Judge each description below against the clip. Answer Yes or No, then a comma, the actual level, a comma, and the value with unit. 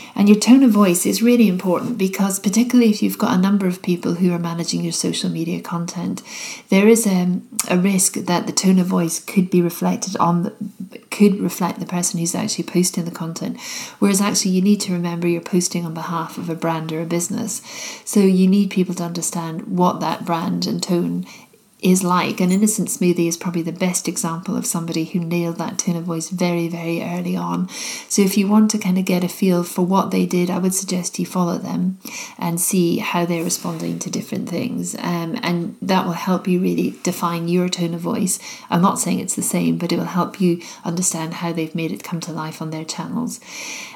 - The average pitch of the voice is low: No, medium, 180 Hz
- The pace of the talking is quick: Yes, fast, 215 wpm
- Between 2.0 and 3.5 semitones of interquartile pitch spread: Yes, average, 2.9 semitones